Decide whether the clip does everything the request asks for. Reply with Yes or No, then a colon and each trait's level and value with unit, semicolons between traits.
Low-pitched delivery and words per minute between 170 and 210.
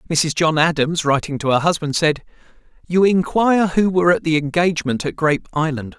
No: medium, 160 Hz; average, 180 wpm